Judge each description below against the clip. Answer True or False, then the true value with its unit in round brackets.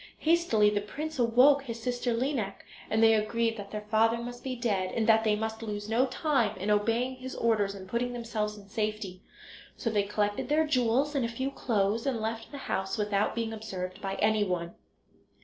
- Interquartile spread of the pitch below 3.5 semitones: True (2.8 semitones)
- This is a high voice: True (225 Hz)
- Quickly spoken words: False (195 wpm)